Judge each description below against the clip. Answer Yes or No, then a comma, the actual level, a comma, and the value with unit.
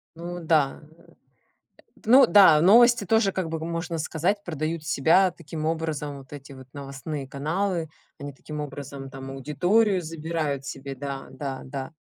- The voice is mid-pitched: Yes, medium, 155 Hz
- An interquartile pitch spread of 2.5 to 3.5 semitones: No, average, 3.9 semitones